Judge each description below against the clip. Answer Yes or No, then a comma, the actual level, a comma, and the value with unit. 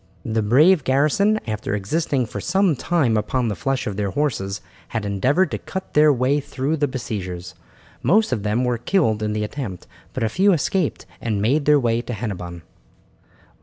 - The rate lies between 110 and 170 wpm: No, average, 180 wpm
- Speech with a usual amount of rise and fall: No, wide, 6.0 semitones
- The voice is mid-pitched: No, low, 125 Hz